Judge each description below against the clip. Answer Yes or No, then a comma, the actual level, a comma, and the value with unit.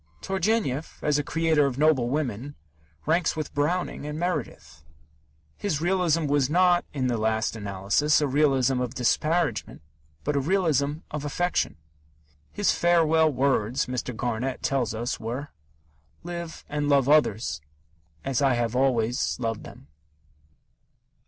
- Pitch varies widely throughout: No, average, 4.4 semitones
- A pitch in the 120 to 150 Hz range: Yes, medium, 140 Hz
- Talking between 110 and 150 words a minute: Yes, slow, 135 wpm